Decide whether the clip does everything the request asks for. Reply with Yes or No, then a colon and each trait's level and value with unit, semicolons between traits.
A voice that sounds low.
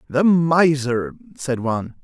No: medium, 145 Hz